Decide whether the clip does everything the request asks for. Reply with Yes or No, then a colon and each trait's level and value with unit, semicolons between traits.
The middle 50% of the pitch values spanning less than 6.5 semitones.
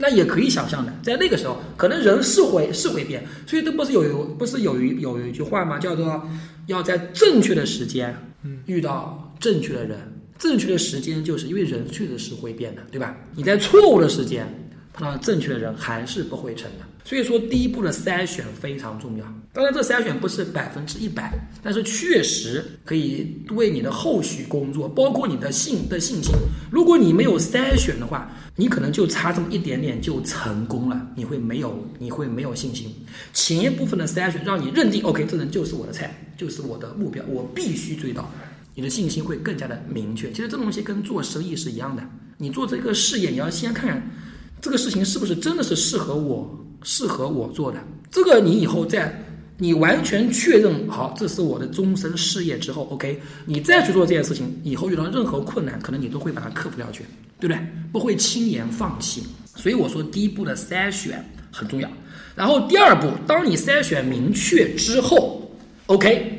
No: wide, 7.4 semitones